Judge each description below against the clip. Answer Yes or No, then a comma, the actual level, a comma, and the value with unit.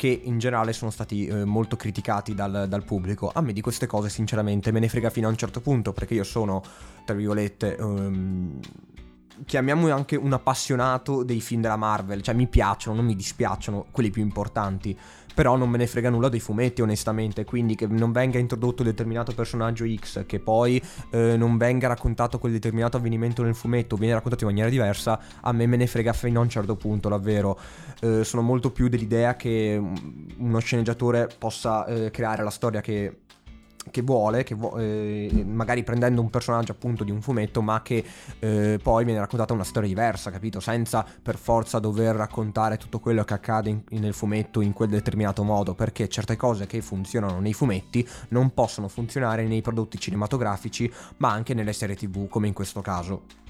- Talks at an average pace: No, fast, 190 wpm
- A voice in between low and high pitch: No, low, 110 Hz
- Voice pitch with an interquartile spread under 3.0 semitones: Yes, narrow, 2.4 semitones